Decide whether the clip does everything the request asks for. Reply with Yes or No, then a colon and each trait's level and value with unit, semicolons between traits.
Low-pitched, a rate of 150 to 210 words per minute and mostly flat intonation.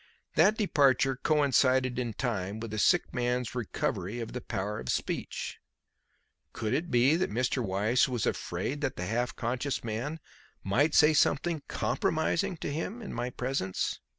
No: low, 125 Hz; average, 155 wpm; average, 4.6 semitones